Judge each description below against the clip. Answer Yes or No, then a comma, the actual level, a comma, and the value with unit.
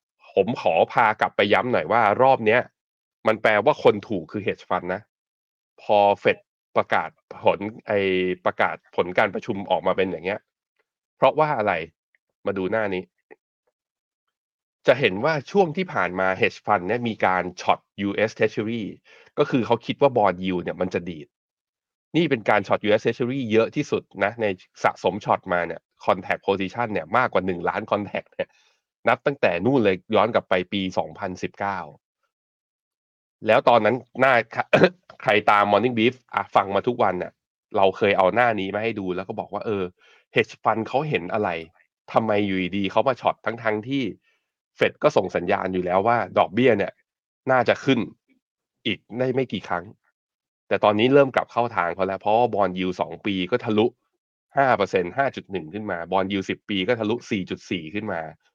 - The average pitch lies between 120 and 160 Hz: No, low, 105 Hz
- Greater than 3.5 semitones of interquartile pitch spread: Yes, average, 4.0 semitones